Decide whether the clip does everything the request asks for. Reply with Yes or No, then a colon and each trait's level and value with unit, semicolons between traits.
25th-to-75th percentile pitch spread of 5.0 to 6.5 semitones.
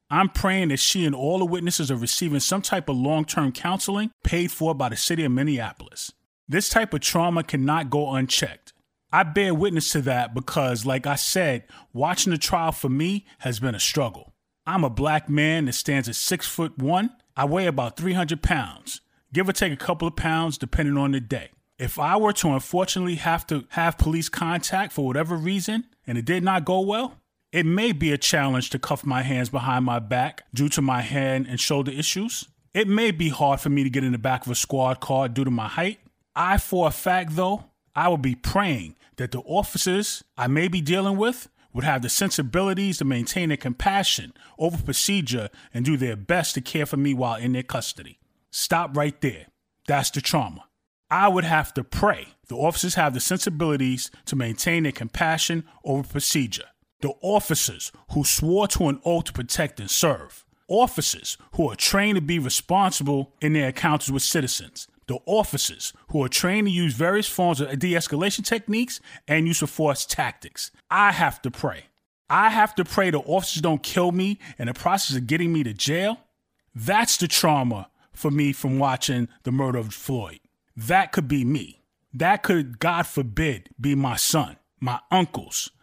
Yes: wide, 5.4 semitones